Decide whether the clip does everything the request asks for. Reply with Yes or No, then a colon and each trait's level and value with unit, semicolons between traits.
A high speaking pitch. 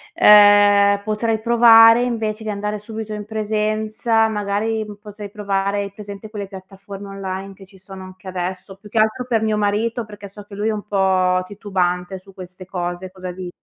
Yes: high, 205 Hz